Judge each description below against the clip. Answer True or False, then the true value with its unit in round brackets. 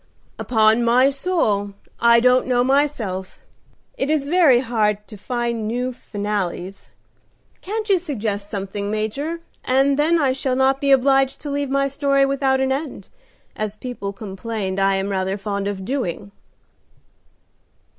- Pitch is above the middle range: True (245 Hz)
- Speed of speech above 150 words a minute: False (140 wpm)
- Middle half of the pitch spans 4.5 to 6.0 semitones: True (5.2 semitones)